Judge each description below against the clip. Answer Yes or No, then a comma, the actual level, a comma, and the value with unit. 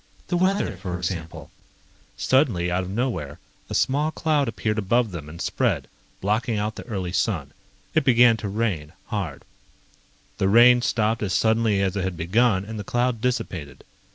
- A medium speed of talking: Yes, average, 170 wpm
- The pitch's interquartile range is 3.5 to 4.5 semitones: No, average, 4.9 semitones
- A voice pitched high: No, low, 105 Hz